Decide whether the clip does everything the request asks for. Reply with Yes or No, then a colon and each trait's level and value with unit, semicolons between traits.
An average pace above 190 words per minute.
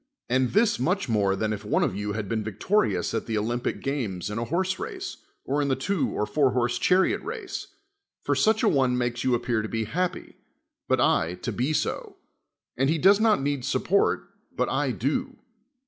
Yes: average, 200 wpm